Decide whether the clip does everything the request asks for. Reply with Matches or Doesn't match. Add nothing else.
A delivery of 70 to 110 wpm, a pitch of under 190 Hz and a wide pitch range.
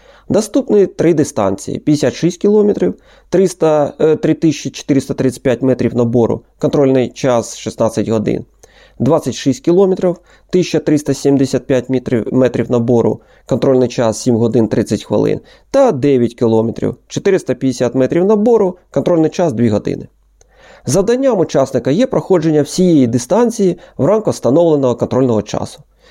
Matches